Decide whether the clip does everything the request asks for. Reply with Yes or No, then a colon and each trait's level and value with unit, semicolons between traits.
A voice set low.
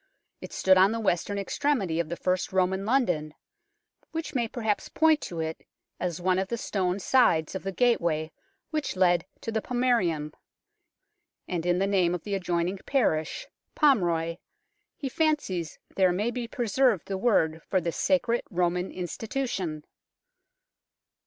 No: high, 190 Hz